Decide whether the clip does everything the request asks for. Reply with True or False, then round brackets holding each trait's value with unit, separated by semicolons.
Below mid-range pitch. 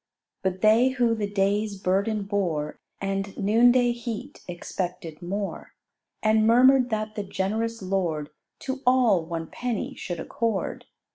False (205 Hz)